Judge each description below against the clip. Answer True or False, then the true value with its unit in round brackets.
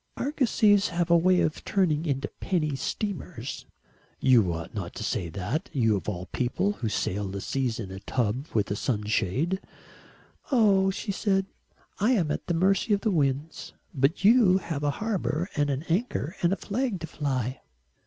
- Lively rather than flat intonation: True (7.6 semitones)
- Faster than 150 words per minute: True (175 wpm)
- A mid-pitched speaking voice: True (155 Hz)